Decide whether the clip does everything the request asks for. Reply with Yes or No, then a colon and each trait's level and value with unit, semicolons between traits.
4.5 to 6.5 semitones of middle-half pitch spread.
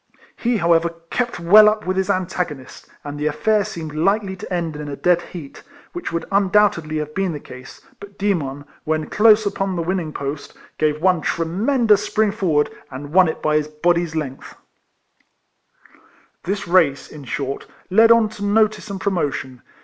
Yes: average, 4.9 semitones